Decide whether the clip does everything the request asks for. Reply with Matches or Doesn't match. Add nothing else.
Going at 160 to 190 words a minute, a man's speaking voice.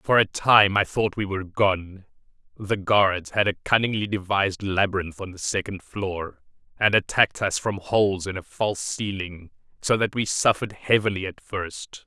Matches